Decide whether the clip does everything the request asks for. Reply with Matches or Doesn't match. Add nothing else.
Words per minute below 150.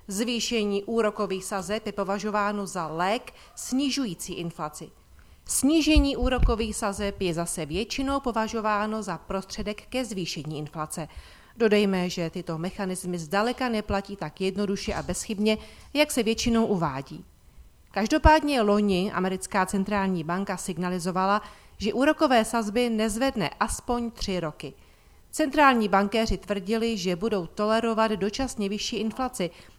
Matches